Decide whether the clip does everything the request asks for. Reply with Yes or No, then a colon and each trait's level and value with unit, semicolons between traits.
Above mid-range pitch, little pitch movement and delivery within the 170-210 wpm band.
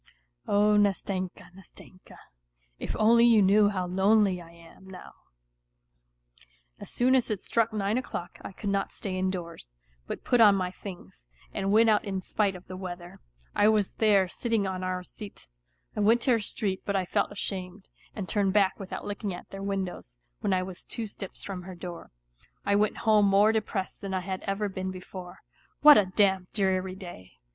Yes: high, 195 Hz; narrow, 2.1 semitones; average, 185 wpm